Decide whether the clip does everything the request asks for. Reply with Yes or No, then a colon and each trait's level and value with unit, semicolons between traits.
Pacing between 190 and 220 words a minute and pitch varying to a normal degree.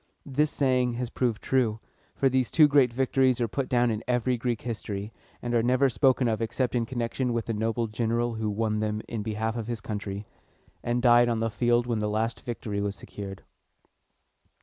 No: average, 195 wpm; narrow, 2.3 semitones